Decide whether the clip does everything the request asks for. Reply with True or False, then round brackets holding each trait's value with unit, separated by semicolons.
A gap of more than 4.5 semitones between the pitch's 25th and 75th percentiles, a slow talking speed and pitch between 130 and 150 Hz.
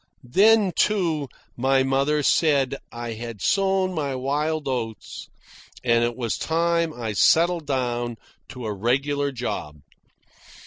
True (5.1 semitones; 125 wpm; 135 Hz)